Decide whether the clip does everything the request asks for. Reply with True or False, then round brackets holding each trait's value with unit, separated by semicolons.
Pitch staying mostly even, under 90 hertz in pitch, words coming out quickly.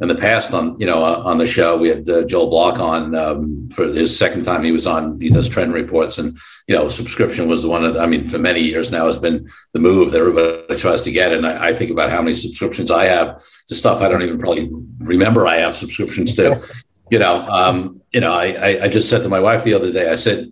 True (0.6 semitones; 80 Hz; 255 wpm)